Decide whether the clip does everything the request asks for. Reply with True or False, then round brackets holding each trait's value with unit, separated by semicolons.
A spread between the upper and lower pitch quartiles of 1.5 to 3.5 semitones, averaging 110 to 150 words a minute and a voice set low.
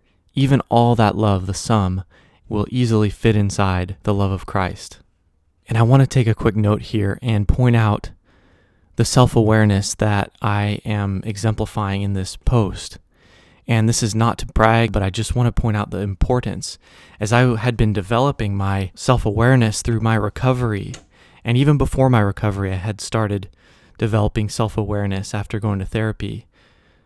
False (2.8 semitones; 170 wpm; 105 Hz)